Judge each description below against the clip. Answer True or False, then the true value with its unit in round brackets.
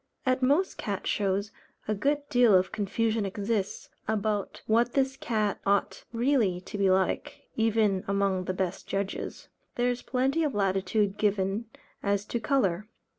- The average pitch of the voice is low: False (210 Hz)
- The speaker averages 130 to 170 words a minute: True (150 wpm)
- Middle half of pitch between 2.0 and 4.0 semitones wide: True (3.5 semitones)